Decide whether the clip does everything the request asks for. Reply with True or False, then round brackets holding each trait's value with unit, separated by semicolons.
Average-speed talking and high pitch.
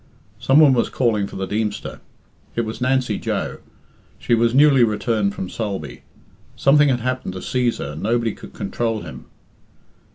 False (160 wpm; 115 Hz)